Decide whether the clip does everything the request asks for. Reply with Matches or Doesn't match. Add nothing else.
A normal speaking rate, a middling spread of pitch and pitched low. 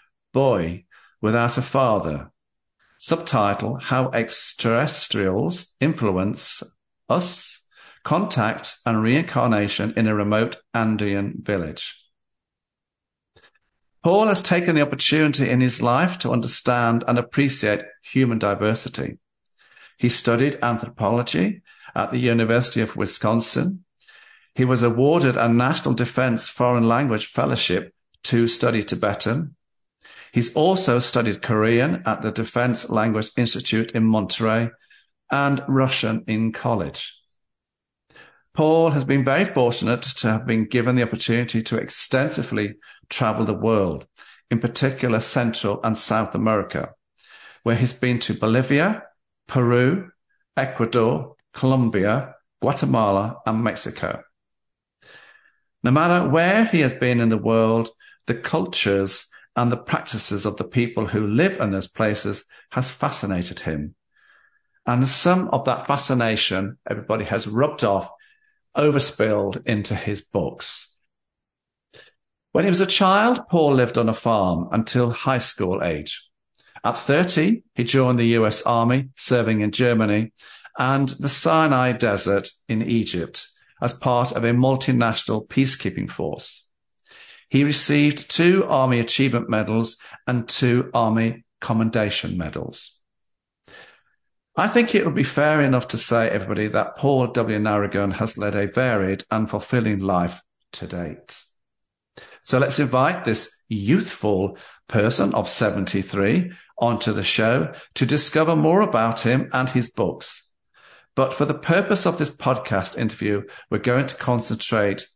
Doesn't match